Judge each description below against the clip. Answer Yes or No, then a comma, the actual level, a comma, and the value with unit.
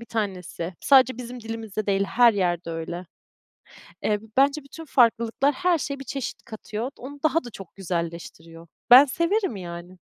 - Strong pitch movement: Yes, wide, 6.9 semitones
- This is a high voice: Yes, high, 225 Hz